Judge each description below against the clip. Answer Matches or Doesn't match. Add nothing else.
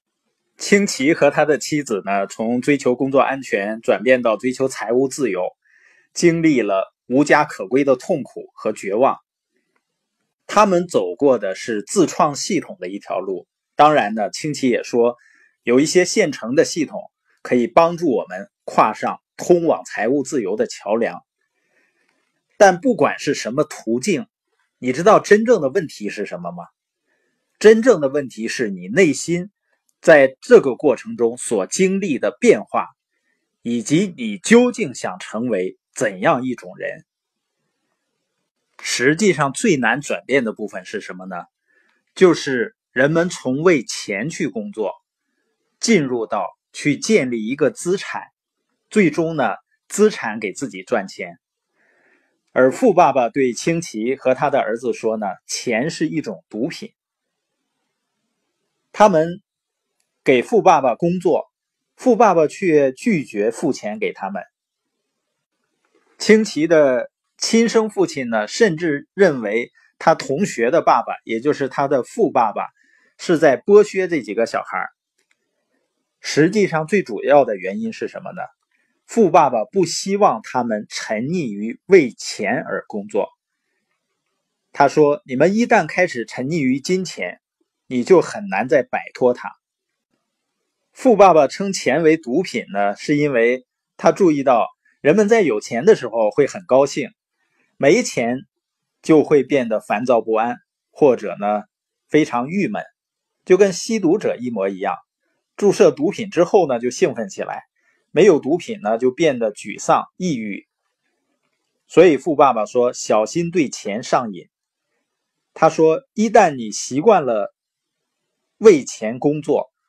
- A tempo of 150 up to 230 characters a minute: Matches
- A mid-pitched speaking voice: Matches